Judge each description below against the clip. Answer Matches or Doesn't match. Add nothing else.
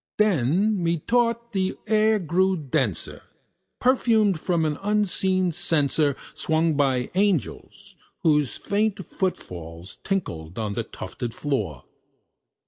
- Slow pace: Matches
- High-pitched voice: Doesn't match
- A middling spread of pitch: Doesn't match